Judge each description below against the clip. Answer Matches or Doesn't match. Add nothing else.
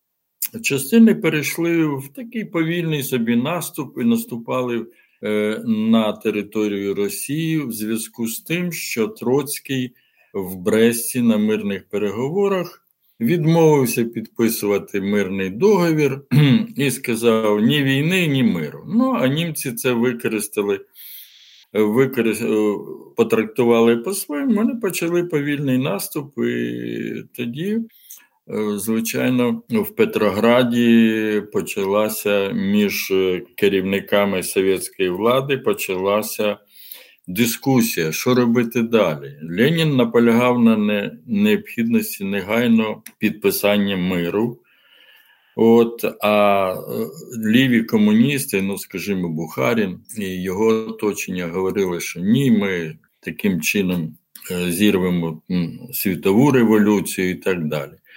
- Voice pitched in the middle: Doesn't match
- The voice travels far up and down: Matches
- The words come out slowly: Matches